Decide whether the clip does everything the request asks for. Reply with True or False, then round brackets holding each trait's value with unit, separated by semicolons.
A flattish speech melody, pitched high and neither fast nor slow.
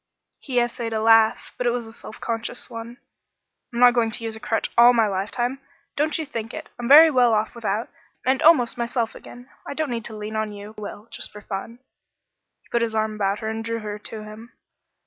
False (2.0 semitones; 230 Hz; 230 wpm)